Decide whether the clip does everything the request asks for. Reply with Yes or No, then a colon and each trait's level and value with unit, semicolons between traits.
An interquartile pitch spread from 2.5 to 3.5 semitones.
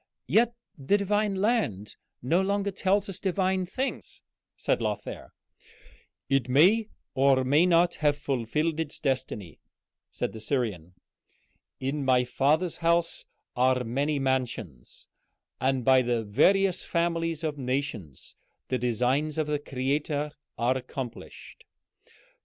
No: average, 5.3 semitones